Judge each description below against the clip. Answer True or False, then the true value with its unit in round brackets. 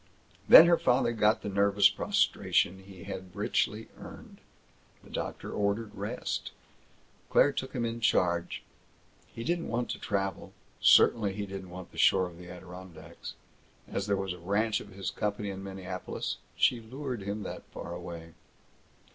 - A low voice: True (100 Hz)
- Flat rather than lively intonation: False (3.2 semitones)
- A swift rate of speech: False (155 wpm)